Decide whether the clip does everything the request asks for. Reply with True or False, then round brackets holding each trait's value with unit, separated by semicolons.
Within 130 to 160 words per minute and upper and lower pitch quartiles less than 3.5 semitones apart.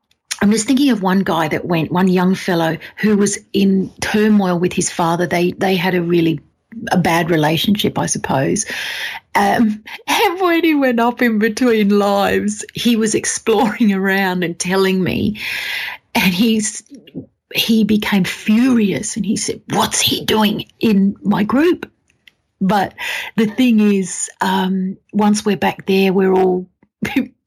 True (150 wpm; 3.1 semitones)